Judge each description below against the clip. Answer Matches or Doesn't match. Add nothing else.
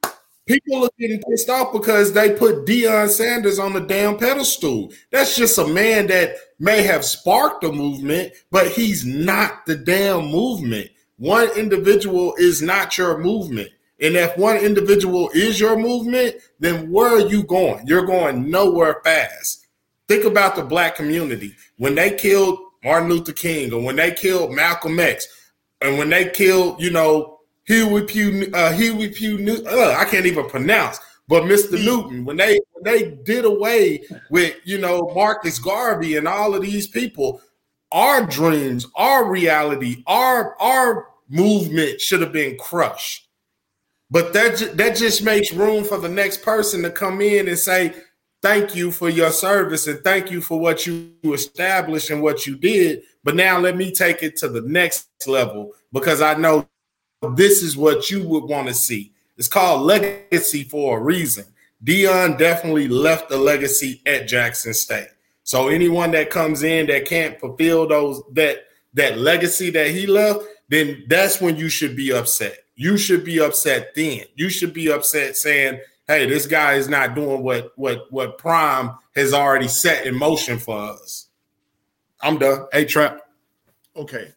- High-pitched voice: Doesn't match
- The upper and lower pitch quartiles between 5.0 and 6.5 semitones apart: Matches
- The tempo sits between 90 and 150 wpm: Doesn't match